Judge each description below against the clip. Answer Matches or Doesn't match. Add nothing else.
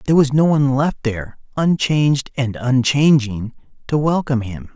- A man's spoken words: Matches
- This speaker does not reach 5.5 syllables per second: Matches